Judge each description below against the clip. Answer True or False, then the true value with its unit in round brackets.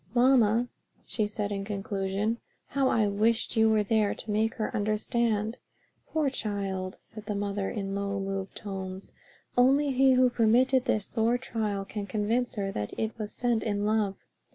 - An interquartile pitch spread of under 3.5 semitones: True (2.7 semitones)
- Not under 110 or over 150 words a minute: False (165 wpm)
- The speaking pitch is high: True (215 Hz)